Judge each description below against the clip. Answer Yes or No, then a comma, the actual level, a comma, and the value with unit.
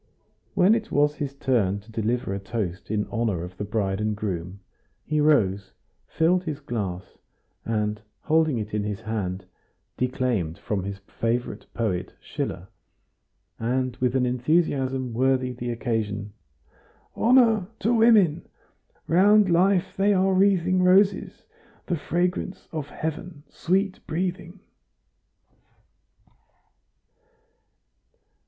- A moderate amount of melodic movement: No, wide, 8.9 semitones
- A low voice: Yes, low, 130 Hz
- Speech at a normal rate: No, slow, 115 wpm